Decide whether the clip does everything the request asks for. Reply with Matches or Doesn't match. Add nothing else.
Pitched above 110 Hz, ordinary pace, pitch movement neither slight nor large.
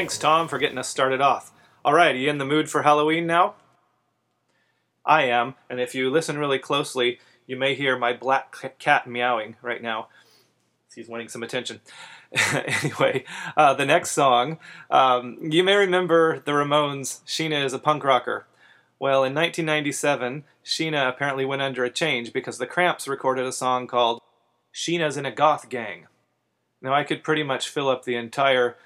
Matches